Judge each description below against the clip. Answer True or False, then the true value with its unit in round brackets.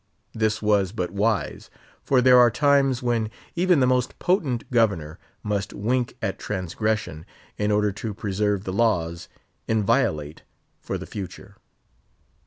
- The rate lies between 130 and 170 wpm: True (135 wpm)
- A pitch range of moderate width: True (3.9 semitones)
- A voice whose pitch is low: True (110 Hz)